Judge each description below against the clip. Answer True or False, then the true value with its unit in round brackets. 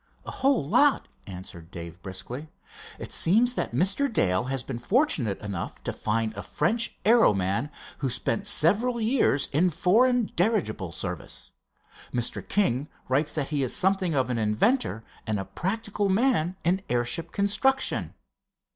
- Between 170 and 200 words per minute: False (145 wpm)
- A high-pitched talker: False (155 Hz)